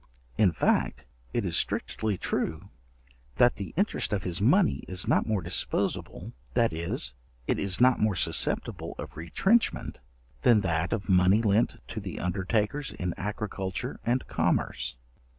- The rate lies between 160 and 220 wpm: No, average, 145 wpm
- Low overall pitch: Yes, low, 100 Hz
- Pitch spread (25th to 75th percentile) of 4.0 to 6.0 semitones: Yes, average, 4.3 semitones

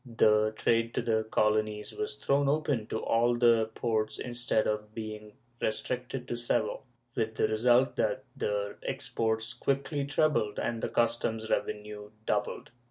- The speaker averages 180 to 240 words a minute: No, average, 145 wpm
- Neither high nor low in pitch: No, low, 115 Hz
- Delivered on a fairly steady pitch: Yes, narrow, 2.3 semitones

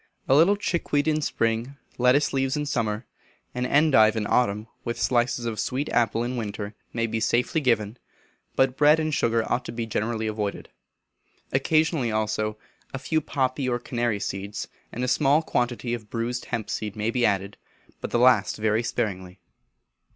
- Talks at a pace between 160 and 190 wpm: Yes, average, 170 wpm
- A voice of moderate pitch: No, low, 120 Hz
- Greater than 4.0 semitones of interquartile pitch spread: No, average, 3.6 semitones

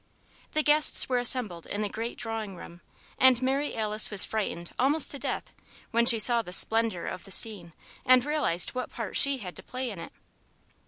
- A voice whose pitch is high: Yes, high, 230 Hz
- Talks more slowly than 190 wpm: No, average, 195 wpm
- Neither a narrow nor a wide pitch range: Yes, average, 4.1 semitones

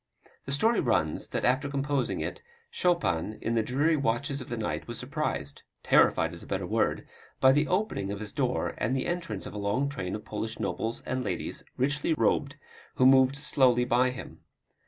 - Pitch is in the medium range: No, low, 130 Hz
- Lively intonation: No, average, 4.5 semitones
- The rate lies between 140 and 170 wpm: No, average, 190 wpm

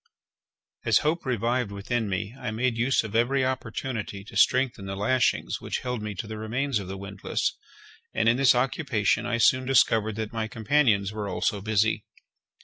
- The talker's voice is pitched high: No, low, 115 Hz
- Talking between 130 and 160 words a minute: No, average, 175 wpm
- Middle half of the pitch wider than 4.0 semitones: No, average, 3.4 semitones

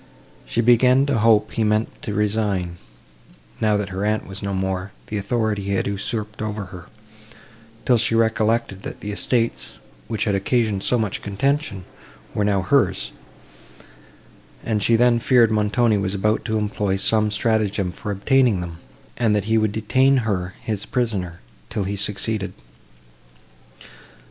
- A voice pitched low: Yes, low, 105 Hz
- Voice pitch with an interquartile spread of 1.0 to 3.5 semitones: Yes, narrow, 2.4 semitones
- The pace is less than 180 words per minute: Yes, average, 155 wpm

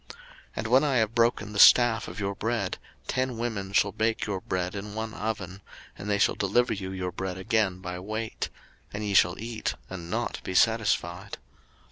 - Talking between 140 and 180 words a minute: No, average, 190 wpm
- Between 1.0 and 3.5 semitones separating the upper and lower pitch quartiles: Yes, average, 2.9 semitones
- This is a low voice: Yes, low, 105 Hz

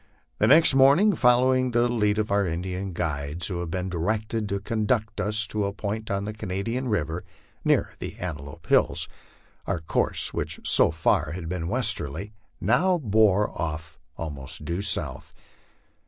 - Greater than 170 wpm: No, average, 160 wpm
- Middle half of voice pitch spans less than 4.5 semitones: No, average, 4.8 semitones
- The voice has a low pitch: Yes, low, 100 Hz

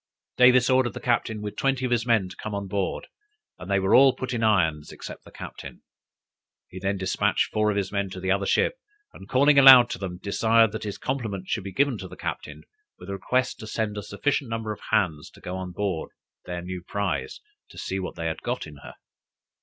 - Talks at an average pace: No, fast, 225 wpm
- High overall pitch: No, low, 105 Hz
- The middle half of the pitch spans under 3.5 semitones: No, average, 4.4 semitones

